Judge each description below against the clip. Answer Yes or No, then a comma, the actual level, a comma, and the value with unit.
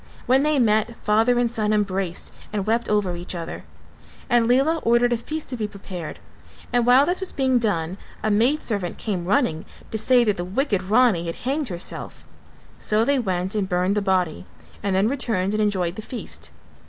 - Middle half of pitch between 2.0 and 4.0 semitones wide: No, average, 4.5 semitones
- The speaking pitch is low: No, high, 215 Hz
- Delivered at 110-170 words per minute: No, average, 190 wpm